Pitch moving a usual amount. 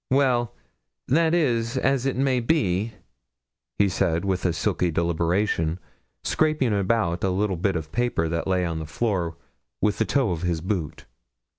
No: wide, 6.1 semitones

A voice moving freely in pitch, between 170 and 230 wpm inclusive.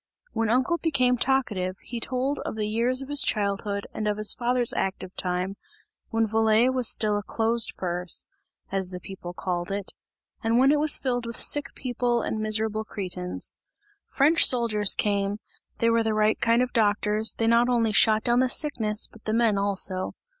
No: average, 3.2 semitones; average, 180 wpm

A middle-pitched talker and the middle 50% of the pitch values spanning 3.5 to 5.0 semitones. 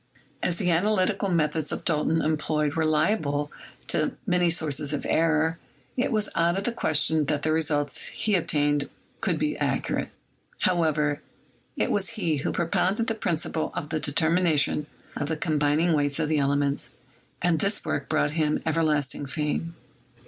No: medium, 160 Hz; average, 2.7 semitones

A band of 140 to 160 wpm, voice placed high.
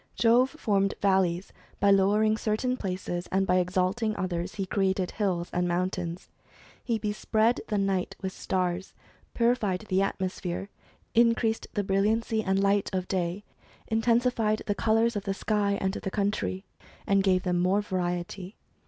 Yes: average, 145 wpm; high, 195 Hz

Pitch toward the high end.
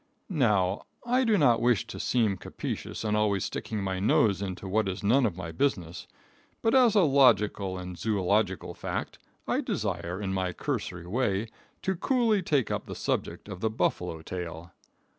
No: low, 105 Hz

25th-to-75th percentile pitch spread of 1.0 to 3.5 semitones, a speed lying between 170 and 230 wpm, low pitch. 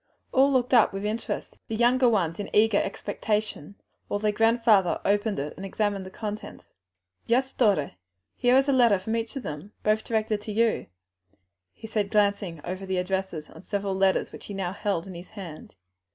No: average, 2.8 semitones; average, 185 wpm; high, 205 Hz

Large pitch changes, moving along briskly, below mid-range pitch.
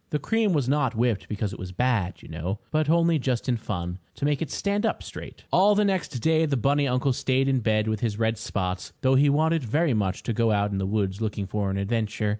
Yes: wide, 6.0 semitones; fast, 245 wpm; low, 120 Hz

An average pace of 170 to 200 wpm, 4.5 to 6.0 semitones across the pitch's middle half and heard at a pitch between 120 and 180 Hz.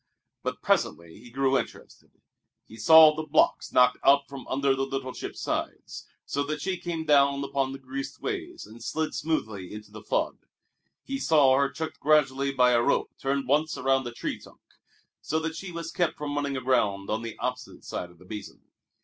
No: average, 190 wpm; average, 3.4 semitones; low, 135 Hz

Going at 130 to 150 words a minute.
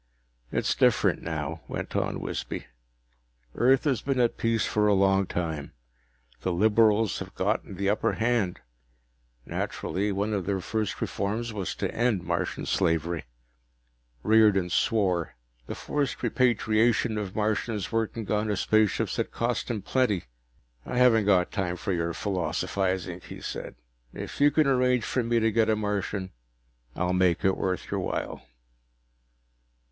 Yes: average, 145 wpm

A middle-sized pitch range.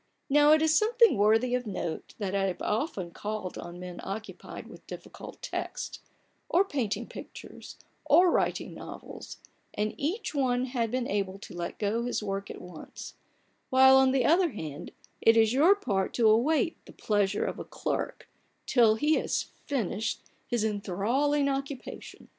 No: wide, 5.7 semitones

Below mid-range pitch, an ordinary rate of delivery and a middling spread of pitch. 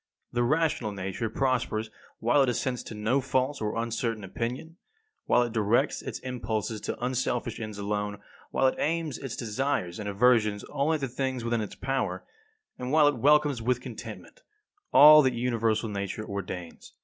Yes: low, 120 Hz; average, 165 wpm; average, 3.7 semitones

